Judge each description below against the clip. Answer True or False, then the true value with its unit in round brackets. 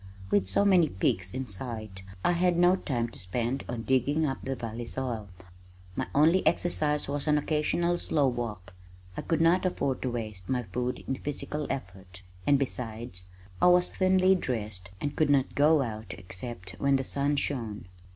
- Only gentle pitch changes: False (5.6 semitones)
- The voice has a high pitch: False (130 Hz)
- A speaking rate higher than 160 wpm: True (175 wpm)